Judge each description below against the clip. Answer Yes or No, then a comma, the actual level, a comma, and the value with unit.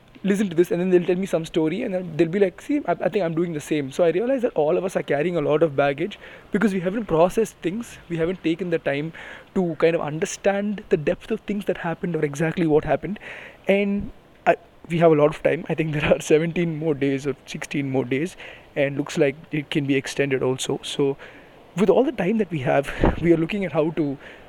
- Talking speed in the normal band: No, fast, 245 wpm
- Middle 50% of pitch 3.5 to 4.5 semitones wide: Yes, average, 3.9 semitones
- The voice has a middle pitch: Yes, medium, 165 Hz